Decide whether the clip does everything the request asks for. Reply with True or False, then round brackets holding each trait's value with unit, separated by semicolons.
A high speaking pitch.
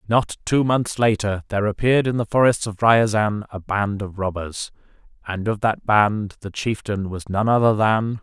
False (105 Hz)